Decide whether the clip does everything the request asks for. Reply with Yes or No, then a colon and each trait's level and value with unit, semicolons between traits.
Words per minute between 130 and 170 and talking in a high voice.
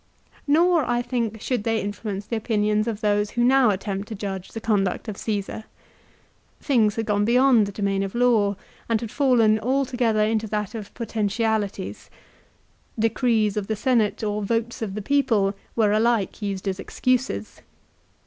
Yes: average, 160 wpm; high, 220 Hz